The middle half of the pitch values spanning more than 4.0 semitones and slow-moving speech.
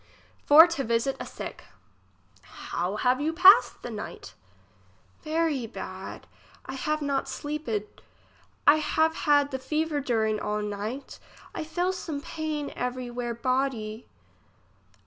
Yes: average, 4.7 semitones; slow, 125 wpm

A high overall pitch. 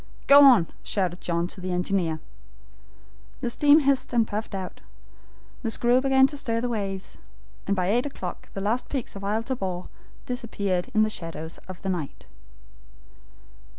Yes: high, 210 Hz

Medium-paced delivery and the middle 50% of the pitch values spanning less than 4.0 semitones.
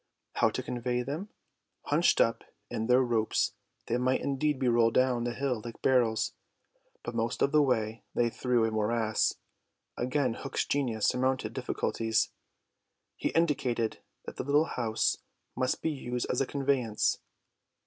Yes: average, 150 wpm; average, 2.7 semitones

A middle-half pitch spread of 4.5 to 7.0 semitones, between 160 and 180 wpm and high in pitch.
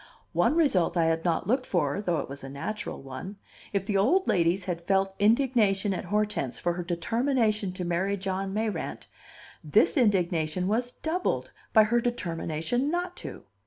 Yes: average, 4.9 semitones; average, 165 wpm; high, 195 Hz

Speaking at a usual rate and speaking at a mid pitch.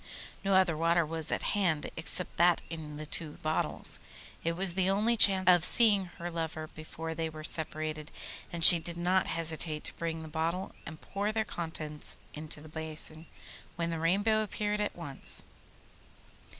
Yes: average, 170 wpm; medium, 165 Hz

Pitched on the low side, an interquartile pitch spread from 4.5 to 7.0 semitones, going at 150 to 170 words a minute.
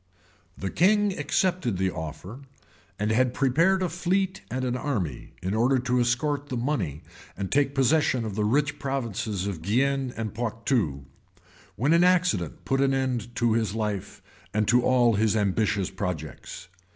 Yes: low, 120 Hz; average, 5.2 semitones; average, 165 wpm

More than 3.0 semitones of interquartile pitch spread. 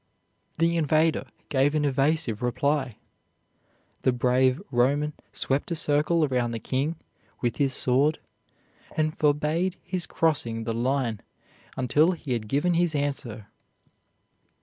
Yes: average, 3.8 semitones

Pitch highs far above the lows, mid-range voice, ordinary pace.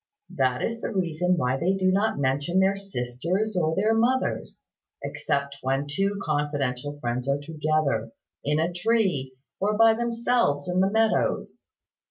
Yes: wide, 6.1 semitones; medium, 170 Hz; average, 150 wpm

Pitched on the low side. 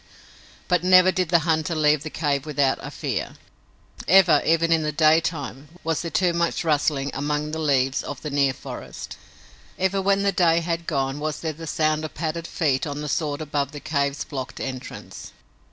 No: medium, 155 Hz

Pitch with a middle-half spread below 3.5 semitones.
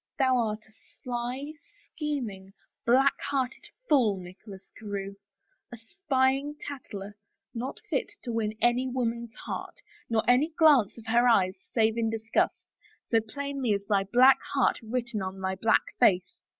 No: average, 3.8 semitones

